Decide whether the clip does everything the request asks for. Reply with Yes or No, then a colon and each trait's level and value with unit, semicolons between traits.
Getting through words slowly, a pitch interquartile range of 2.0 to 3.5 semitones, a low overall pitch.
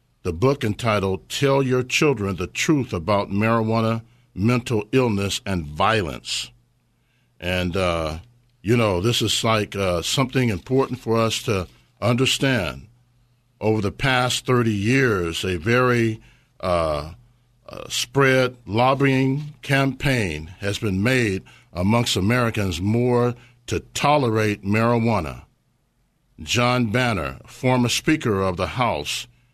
No: slow, 115 wpm; average, 4.0 semitones; low, 115 Hz